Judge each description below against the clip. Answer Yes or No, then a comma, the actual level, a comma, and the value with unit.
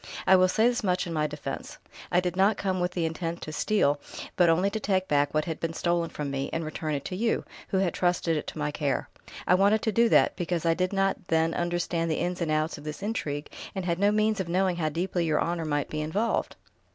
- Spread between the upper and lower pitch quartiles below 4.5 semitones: Yes, average, 3.5 semitones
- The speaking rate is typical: No, fast, 250 wpm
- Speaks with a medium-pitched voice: Yes, medium, 175 Hz